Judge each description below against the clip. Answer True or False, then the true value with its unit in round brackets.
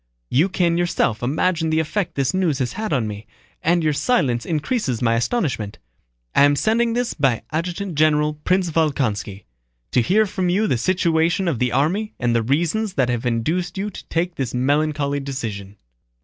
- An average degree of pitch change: False (6.4 semitones)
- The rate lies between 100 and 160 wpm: False (175 wpm)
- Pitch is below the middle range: False (155 Hz)